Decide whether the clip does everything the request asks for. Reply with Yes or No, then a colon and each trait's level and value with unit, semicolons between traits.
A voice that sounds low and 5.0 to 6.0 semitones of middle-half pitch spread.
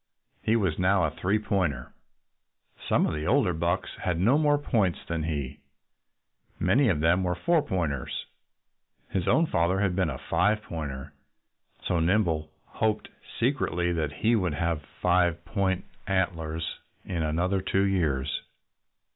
No: very low, 90 Hz; average, 3.6 semitones